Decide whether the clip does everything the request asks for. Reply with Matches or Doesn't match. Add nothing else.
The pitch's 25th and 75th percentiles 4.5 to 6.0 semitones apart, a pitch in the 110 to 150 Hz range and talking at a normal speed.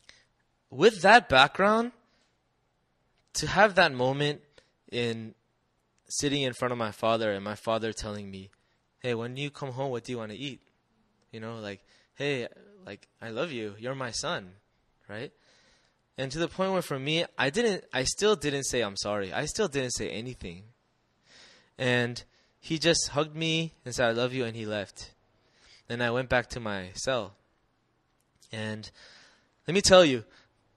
Matches